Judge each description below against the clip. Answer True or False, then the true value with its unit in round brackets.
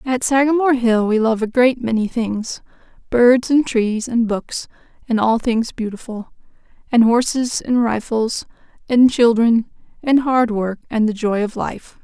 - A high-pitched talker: True (235 Hz)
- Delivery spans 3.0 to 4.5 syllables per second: True (4.3 syllables/s)